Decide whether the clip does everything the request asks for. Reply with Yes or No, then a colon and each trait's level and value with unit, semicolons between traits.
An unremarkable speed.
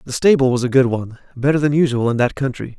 No: fast, 260 wpm